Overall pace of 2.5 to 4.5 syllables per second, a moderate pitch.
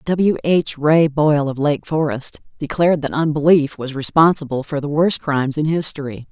No: 5.0 syllables/s; medium, 150 Hz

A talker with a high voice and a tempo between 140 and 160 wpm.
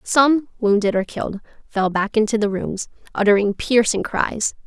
Yes: high, 215 Hz; average, 155 wpm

